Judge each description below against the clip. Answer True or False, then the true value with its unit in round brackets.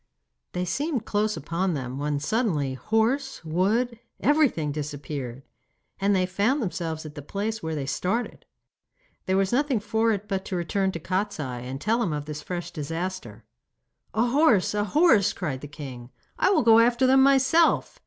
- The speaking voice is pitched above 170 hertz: True (190 Hz)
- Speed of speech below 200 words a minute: True (170 wpm)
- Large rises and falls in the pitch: True (7.3 semitones)